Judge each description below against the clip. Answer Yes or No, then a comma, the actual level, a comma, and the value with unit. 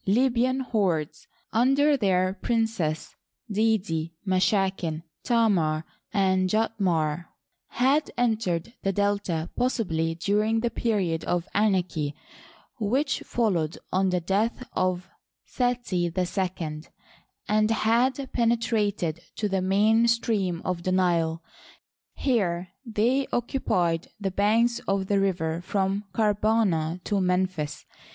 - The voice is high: Yes, high, 195 Hz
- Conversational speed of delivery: No, slow, 105 wpm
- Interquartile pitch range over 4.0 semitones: Yes, average, 4.5 semitones